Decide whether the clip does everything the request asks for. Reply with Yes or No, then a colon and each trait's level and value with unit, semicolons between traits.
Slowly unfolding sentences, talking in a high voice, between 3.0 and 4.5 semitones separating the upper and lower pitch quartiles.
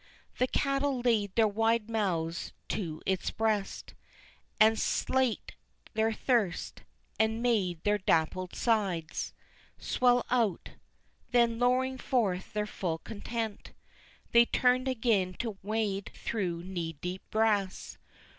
Yes: slow, 115 wpm; high, 215 Hz; average, 4.0 semitones